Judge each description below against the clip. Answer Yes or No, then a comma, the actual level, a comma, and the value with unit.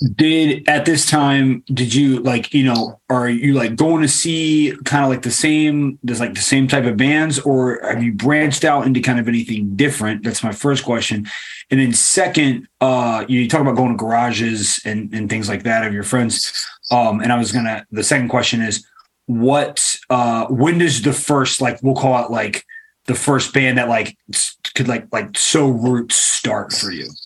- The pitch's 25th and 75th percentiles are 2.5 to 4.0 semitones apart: Yes, average, 3.3 semitones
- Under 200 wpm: No, fast, 205 wpm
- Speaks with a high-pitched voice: No, low, 125 Hz